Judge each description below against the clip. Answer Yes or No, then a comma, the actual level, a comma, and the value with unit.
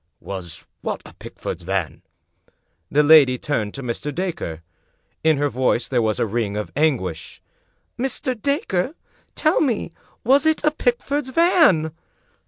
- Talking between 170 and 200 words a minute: No, average, 140 wpm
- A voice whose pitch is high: No, medium, 150 Hz